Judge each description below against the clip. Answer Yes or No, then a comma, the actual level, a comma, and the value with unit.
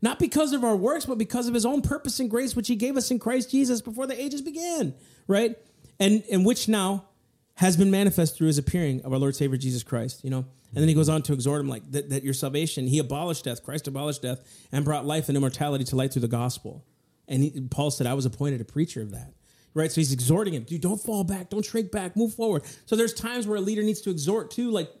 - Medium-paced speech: No, fast, 260 wpm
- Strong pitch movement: Yes, wide, 8.4 semitones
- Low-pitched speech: No, medium, 160 Hz